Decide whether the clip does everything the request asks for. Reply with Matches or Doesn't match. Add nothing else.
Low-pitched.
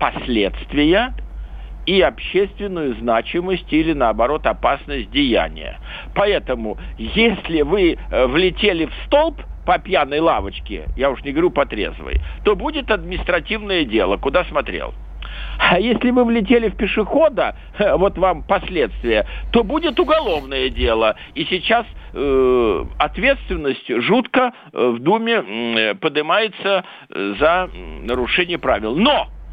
Doesn't match